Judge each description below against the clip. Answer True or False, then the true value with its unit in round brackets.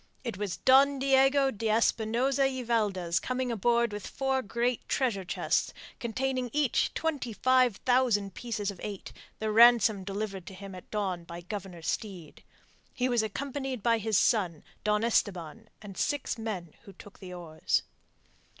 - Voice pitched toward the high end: True (220 Hz)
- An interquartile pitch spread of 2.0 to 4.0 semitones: False (4.6 semitones)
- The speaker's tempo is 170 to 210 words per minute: False (160 wpm)